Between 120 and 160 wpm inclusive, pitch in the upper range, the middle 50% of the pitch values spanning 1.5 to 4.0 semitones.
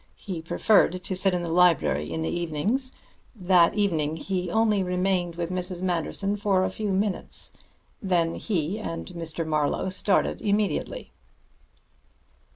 No: average, 140 wpm; medium, 180 Hz; average, 3.1 semitones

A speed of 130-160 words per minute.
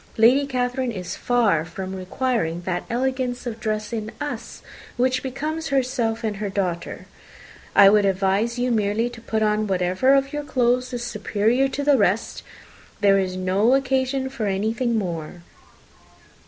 Yes: average, 150 wpm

